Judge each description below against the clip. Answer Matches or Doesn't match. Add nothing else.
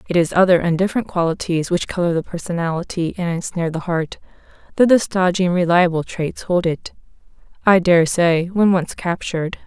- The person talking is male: Doesn't match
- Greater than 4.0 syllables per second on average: Matches